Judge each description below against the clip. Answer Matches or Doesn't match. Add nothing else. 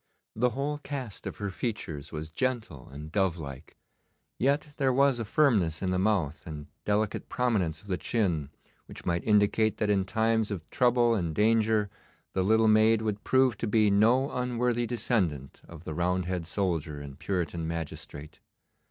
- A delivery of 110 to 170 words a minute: Matches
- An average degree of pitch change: Doesn't match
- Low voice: Matches